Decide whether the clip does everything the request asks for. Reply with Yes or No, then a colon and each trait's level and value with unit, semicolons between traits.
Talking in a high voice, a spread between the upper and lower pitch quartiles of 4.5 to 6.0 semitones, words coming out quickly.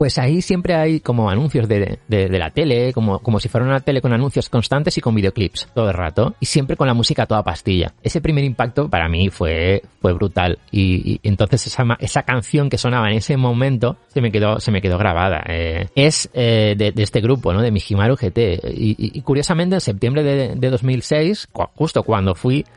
No: low, 120 Hz; average, 4.9 semitones; fast, 215 wpm